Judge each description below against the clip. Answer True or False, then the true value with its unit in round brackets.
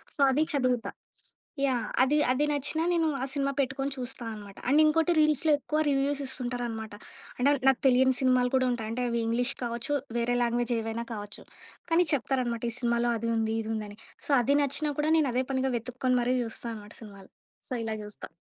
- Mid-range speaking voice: False (250 Hz)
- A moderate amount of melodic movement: True (3.1 semitones)